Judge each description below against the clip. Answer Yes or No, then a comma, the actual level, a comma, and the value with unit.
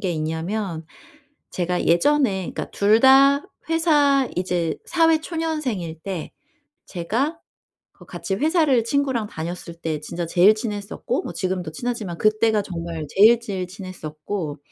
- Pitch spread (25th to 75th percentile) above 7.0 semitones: Yes, wide, 7.5 semitones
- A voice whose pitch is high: Yes, high, 200 Hz